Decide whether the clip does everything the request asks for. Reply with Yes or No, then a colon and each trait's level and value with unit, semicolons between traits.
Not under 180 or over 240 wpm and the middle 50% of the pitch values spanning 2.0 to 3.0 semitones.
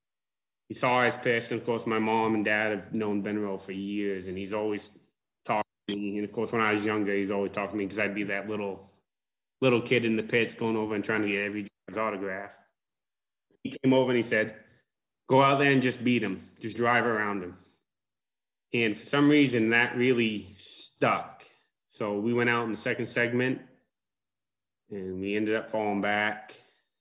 Yes: average, 200 wpm; average, 2.7 semitones